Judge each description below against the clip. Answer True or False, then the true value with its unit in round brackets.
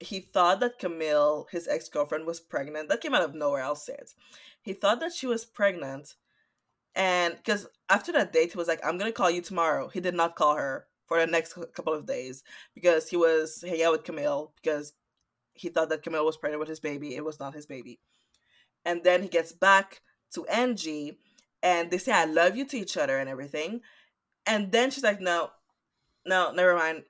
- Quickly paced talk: True (215 wpm)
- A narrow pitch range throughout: False (3.7 semitones)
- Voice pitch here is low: False (170 Hz)